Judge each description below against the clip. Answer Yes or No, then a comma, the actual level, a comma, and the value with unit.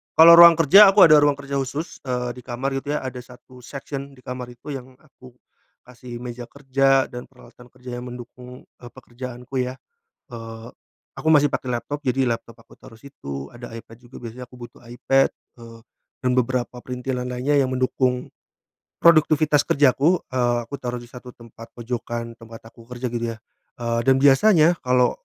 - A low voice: Yes, low, 125 Hz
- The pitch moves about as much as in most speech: No, narrow, 2.3 semitones